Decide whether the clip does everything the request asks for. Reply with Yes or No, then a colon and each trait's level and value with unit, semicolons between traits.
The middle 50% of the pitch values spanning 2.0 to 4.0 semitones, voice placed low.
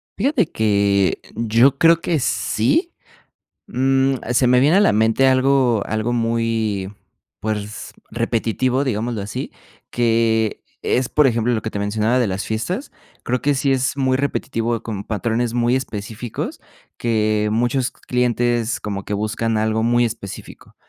Yes: average, 3.0 semitones; low, 115 Hz